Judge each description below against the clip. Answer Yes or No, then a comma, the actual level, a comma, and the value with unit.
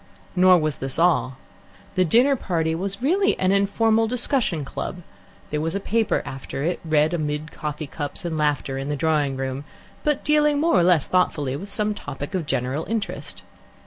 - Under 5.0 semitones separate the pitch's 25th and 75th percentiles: No, wide, 5.6 semitones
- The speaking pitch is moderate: Yes, medium, 170 Hz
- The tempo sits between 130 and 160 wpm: No, average, 175 wpm